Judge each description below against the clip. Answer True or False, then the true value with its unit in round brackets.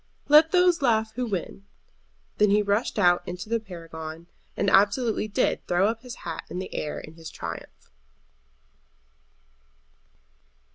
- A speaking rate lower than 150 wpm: True (140 wpm)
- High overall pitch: True (205 Hz)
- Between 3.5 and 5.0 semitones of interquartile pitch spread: True (4.7 semitones)